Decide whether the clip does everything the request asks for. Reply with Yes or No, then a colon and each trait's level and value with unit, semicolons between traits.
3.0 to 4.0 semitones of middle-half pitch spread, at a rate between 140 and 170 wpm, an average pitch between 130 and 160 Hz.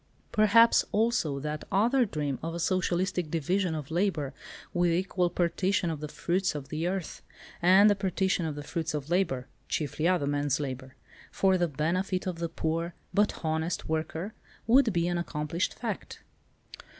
No: average, 3.7 semitones; average, 160 wpm; medium, 170 Hz